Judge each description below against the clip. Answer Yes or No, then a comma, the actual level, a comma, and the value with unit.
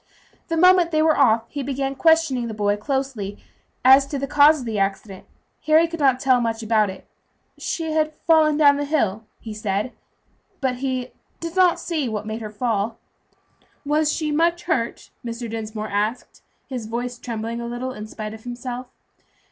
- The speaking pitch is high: Yes, very high, 250 Hz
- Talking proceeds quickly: No, average, 180 wpm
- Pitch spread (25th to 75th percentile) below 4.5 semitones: No, wide, 5.4 semitones